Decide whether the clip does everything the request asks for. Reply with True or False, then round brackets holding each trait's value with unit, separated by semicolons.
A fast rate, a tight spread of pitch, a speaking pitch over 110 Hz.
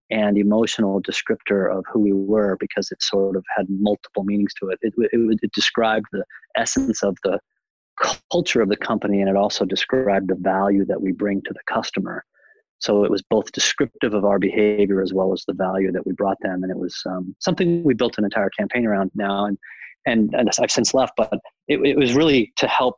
False (220 wpm; 1.8 semitones; 100 Hz)